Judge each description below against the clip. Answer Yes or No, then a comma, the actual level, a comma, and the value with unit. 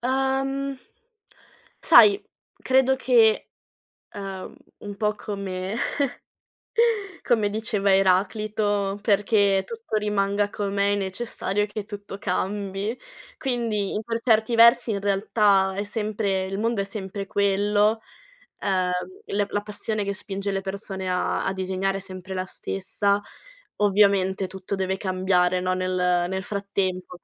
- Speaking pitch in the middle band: No, high, 200 Hz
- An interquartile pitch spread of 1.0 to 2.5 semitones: Yes, narrow, 1.9 semitones